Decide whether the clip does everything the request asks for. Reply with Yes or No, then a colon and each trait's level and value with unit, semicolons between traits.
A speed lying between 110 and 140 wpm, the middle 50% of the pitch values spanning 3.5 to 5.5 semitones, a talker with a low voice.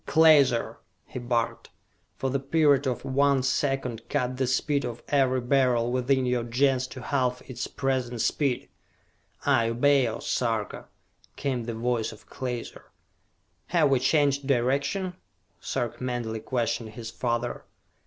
No: slow, 135 wpm; narrow, 2.4 semitones; low, 130 Hz